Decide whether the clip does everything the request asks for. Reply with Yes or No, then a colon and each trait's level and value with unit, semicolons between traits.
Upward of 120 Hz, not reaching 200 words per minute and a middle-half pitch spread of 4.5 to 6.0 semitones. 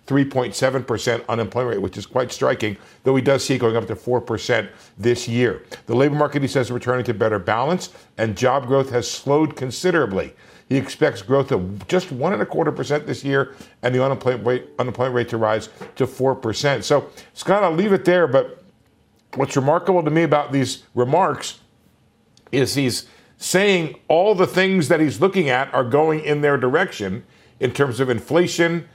No: low, 135 Hz; average, 190 wpm; average, 3.6 semitones